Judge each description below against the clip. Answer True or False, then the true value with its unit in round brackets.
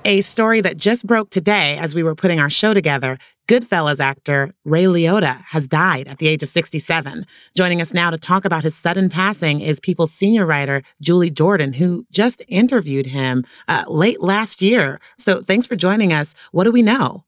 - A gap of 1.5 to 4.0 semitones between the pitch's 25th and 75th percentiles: False (4.8 semitones)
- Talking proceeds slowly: False (195 wpm)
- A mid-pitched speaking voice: True (175 Hz)